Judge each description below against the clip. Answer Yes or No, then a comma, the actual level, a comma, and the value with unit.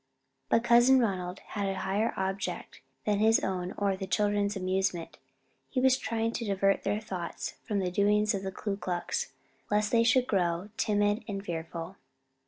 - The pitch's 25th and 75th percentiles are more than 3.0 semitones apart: No, narrow, 2.4 semitones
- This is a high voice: Yes, high, 200 Hz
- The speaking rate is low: No, average, 170 wpm